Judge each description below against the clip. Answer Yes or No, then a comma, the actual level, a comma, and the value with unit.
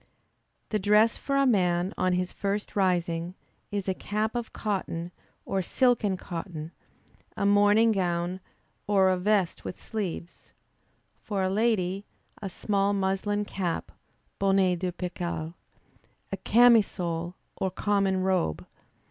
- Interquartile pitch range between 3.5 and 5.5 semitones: No, narrow, 2.5 semitones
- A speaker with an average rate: No, slow, 130 wpm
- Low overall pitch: No, high, 190 Hz